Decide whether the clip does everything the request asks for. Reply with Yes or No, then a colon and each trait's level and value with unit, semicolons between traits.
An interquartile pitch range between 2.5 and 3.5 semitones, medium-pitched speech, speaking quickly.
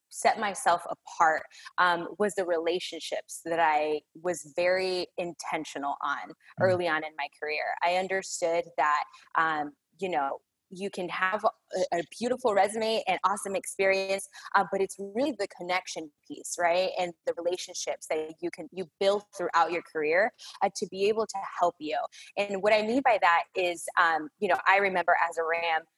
No: average, 2.8 semitones; medium, 180 Hz; average, 175 wpm